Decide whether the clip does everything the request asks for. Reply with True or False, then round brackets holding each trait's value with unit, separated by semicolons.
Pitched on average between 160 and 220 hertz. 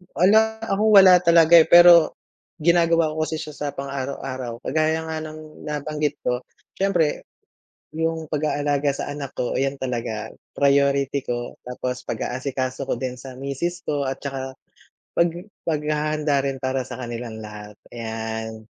False (140 Hz)